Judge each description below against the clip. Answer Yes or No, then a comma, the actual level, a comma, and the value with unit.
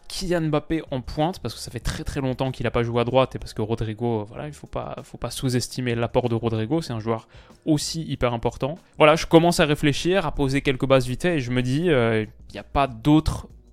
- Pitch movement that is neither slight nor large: Yes, average, 4.2 semitones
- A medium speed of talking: No, fast, 255 wpm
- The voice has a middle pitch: No, low, 130 Hz